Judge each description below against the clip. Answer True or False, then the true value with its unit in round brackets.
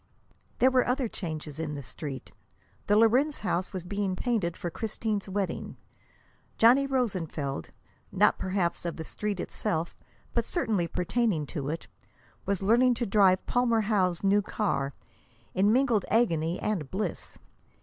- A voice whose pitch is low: False (200 Hz)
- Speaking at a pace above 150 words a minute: False (140 wpm)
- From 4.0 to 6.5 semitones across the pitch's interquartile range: True (5.0 semitones)